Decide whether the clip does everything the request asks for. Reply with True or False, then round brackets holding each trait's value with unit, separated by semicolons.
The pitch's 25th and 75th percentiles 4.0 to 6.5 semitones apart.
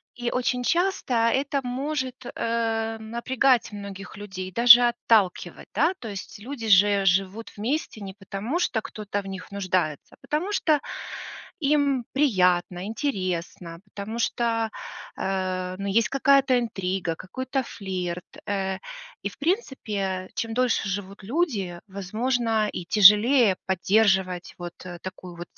True (4.7 semitones)